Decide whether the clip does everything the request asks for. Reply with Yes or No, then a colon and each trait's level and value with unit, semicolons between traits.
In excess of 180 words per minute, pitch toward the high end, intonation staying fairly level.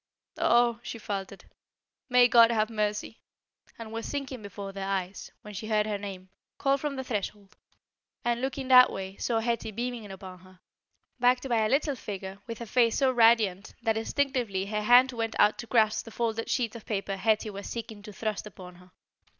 No: average, 190 wpm; high, 220 Hz; average, 3.1 semitones